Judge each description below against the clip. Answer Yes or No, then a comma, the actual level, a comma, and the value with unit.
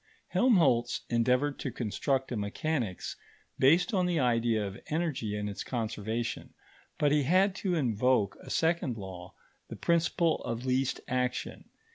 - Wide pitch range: Yes, wide, 6.1 semitones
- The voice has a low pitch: Yes, low, 125 Hz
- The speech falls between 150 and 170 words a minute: No, average, 140 wpm